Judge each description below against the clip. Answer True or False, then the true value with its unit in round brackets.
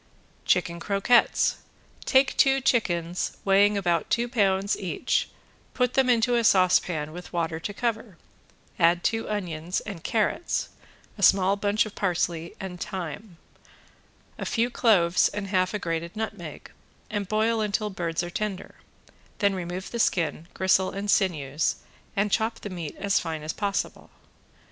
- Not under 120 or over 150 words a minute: True (145 wpm)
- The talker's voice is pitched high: True (195 Hz)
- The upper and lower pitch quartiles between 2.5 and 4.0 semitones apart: True (3.7 semitones)